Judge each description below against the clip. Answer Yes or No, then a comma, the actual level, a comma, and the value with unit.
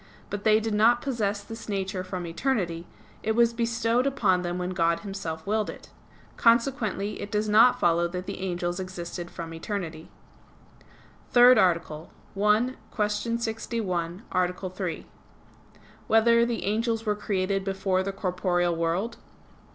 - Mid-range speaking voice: No, high, 200 Hz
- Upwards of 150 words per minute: No, average, 145 wpm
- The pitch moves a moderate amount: Yes, average, 4.0 semitones